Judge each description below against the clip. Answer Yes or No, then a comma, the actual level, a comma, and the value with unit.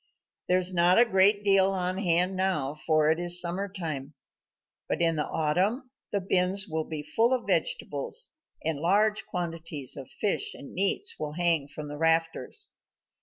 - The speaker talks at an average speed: Yes, average, 170 wpm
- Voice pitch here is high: No, medium, 175 Hz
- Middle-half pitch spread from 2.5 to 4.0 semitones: Yes, average, 3.6 semitones